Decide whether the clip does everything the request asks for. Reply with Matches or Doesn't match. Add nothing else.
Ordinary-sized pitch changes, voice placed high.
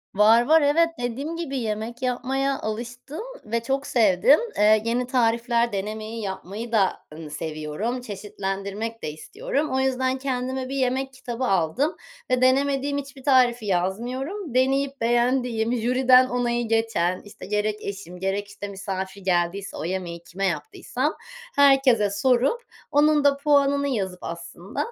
Matches